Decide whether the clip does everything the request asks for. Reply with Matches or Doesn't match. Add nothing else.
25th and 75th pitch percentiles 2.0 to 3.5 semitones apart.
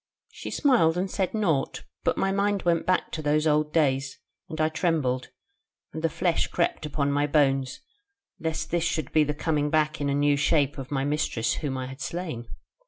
Matches